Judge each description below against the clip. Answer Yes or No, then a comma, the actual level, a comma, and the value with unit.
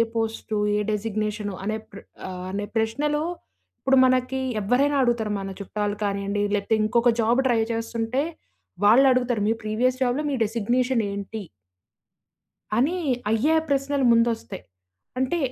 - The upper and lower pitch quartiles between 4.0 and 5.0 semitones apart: No, average, 3.5 semitones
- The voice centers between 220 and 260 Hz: Yes, high, 225 Hz